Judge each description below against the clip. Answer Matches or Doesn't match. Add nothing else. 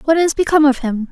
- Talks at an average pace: Doesn't match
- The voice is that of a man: Doesn't match